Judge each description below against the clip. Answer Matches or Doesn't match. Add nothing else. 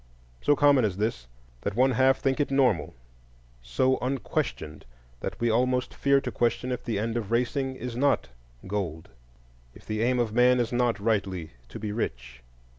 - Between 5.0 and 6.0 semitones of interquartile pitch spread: Doesn't match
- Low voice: Matches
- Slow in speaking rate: Doesn't match